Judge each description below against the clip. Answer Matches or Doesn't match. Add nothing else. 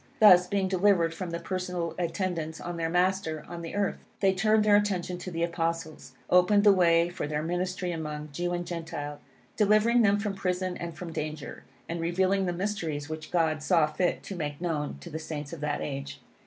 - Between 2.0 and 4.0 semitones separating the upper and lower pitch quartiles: Matches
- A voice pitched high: Doesn't match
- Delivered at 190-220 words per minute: Matches